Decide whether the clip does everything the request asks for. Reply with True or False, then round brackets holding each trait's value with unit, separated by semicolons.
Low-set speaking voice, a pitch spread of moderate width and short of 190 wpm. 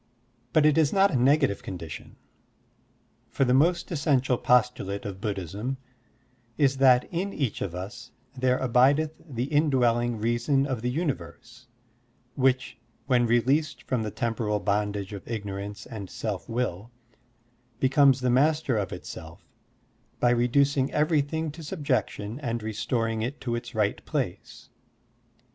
True (125 Hz; 4.2 semitones; 140 wpm)